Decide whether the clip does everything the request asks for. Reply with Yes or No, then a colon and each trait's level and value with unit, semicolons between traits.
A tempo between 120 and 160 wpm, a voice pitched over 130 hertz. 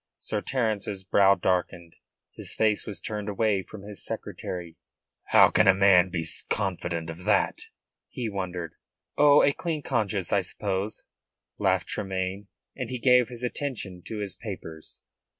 No: average, 150 wpm; low, 100 Hz